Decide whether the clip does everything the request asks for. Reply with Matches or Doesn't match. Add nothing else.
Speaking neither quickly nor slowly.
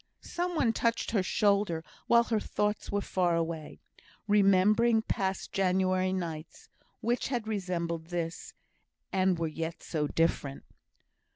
Doesn't match